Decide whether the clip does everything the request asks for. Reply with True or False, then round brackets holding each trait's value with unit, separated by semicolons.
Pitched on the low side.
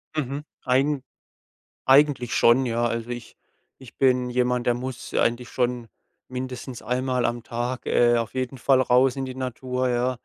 True (125 Hz)